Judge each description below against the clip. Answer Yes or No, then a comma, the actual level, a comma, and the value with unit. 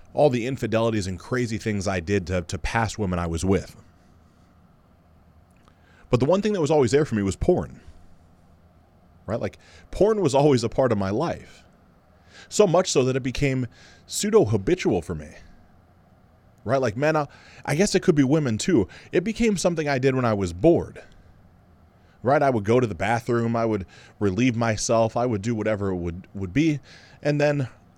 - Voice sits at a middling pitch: No, low, 105 Hz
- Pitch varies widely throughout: Yes, wide, 6.6 semitones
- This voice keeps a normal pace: Yes, average, 190 wpm